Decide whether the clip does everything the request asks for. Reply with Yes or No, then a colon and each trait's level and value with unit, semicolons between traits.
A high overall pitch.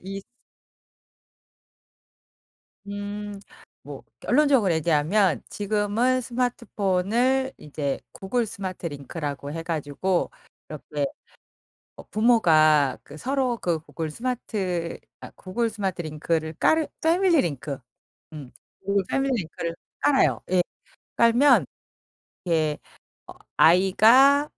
Yes: high, 195 Hz